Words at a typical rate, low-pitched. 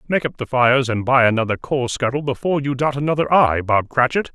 No: fast, 220 wpm; low, 130 Hz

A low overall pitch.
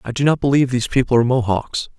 Yes: low, 125 Hz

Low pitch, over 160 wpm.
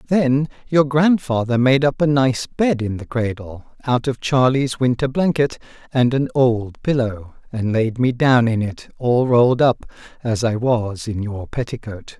Yes: low, 125 Hz; average, 170 wpm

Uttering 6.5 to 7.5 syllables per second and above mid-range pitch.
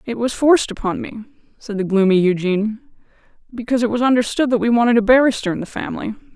Yes: 7.1 syllables/s; high, 230 Hz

